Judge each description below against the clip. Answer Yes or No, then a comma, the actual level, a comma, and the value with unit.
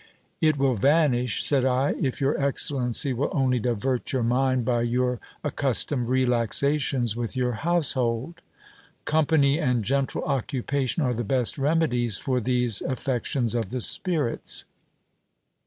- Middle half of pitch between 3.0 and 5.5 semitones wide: No, narrow, 2.6 semitones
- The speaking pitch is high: No, low, 130 Hz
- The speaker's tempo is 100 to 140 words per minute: Yes, slow, 135 wpm